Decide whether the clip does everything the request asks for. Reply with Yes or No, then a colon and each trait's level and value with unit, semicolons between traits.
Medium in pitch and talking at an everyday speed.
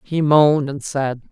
Yes: medium, 145 Hz; average, 180 wpm